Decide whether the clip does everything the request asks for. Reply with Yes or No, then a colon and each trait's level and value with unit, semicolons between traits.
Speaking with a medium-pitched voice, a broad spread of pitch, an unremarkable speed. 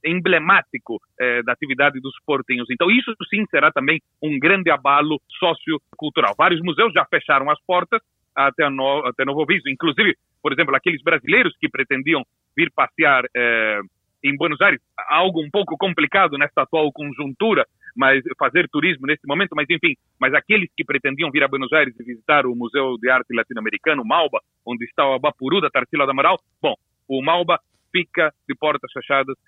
No: medium, 150 Hz; average, 4.2 semitones; average, 175 wpm